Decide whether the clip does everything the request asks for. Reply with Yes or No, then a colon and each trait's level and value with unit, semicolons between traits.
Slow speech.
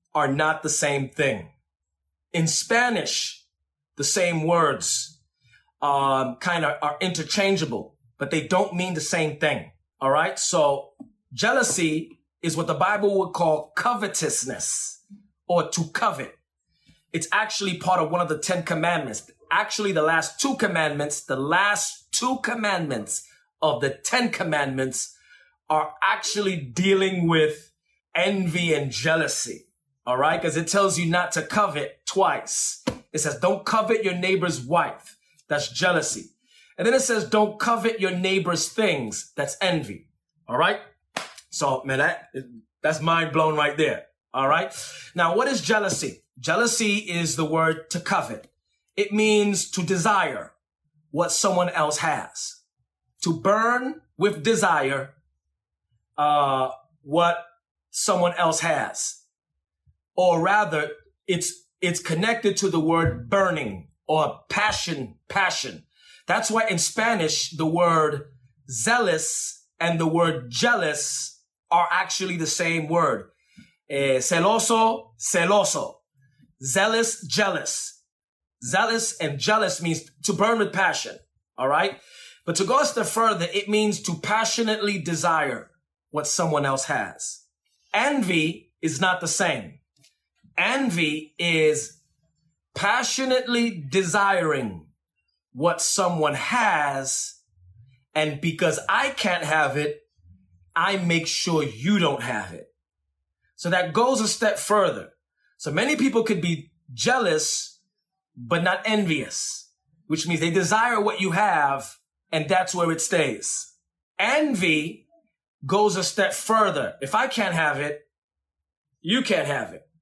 Yes: slow, 130 wpm